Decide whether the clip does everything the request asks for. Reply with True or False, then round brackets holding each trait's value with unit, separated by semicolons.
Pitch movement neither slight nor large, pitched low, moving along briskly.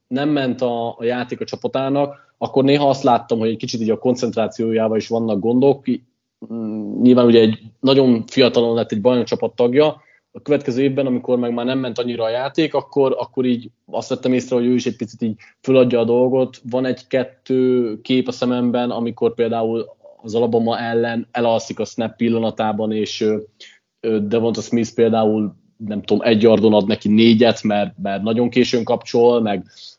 False (2.1 semitones; 120 Hz; 170 wpm)